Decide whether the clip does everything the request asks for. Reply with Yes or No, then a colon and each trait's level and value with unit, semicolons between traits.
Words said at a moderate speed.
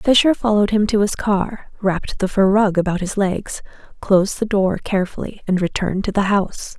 Yes: average, 195 wpm